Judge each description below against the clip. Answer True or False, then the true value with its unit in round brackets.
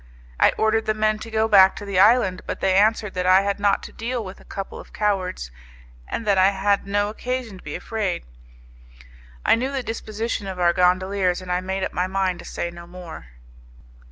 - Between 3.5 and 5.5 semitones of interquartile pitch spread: False (2.7 semitones)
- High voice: True (195 Hz)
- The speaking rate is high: True (215 wpm)